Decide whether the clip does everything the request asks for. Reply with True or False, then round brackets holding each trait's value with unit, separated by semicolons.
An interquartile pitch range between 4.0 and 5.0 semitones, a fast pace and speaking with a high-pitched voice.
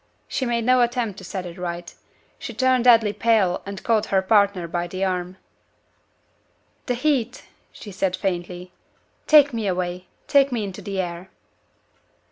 False (4.7 semitones; 155 wpm; 200 Hz)